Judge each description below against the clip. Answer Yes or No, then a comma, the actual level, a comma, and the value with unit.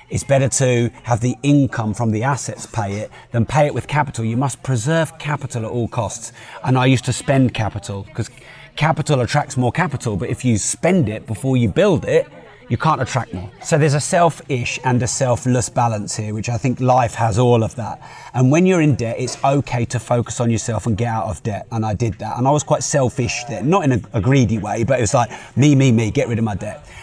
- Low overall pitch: Yes, low, 125 Hz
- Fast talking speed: Yes, fast, 240 wpm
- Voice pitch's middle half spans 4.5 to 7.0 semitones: No, average, 3.2 semitones